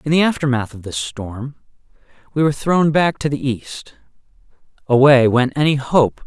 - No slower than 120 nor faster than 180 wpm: Yes, average, 170 wpm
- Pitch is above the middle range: No, low, 135 Hz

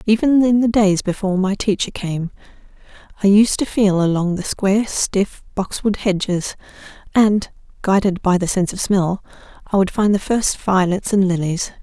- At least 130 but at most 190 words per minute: Yes, average, 160 wpm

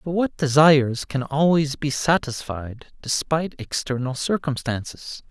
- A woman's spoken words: No, male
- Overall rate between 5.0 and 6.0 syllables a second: No, 4.5 syllables/s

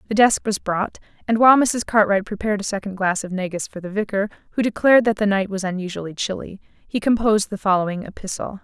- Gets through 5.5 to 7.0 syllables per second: Yes, 6.4 syllables/s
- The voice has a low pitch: No, high, 205 Hz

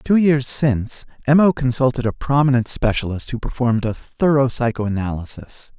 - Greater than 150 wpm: No, average, 145 wpm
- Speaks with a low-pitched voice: Yes, low, 125 Hz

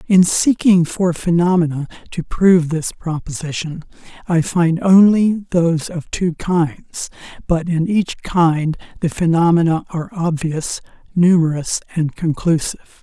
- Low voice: No, medium, 170 Hz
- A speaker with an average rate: No, slow, 120 wpm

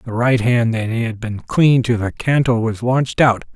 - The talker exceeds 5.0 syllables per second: No, 4.7 syllables/s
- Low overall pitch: Yes, low, 120 Hz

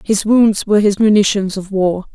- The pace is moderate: Yes, average, 195 wpm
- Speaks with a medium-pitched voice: No, high, 205 Hz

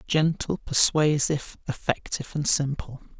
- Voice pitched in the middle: Yes, medium, 145 Hz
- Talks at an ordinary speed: No, slow, 95 wpm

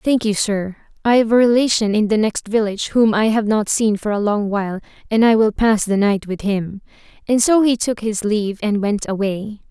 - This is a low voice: No, high, 215 Hz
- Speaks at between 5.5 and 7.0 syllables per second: No, 5.3 syllables/s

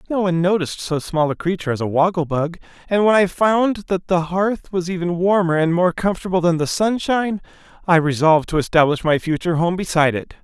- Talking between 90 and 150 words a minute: No, fast, 205 wpm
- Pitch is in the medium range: Yes, medium, 175 Hz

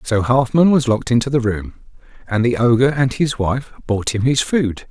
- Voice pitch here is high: No, low, 125 Hz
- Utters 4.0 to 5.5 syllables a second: Yes, 5.1 syllables/s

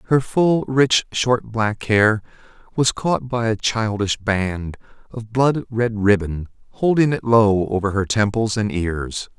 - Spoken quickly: No, average, 155 wpm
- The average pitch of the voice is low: Yes, low, 110 Hz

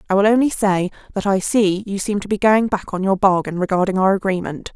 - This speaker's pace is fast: Yes, fast, 240 wpm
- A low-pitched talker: No, high, 195 Hz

